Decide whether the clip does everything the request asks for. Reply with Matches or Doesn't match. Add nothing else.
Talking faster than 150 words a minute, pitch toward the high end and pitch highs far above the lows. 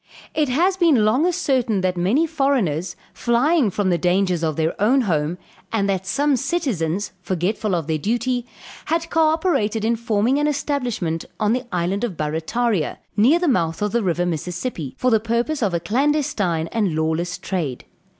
Matches